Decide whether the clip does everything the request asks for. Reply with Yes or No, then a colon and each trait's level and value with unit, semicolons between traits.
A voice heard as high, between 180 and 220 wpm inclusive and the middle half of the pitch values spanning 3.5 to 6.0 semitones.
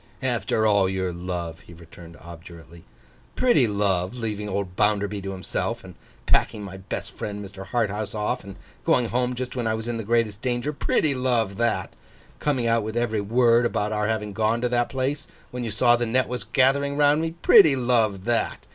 No: low, 110 Hz; average, 190 wpm; average, 3.8 semitones